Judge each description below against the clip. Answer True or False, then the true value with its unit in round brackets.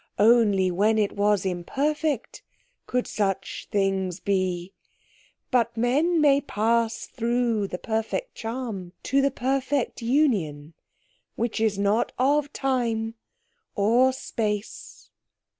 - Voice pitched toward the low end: False (225 Hz)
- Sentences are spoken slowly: True (110 wpm)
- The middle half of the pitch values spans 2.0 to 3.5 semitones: False (4.5 semitones)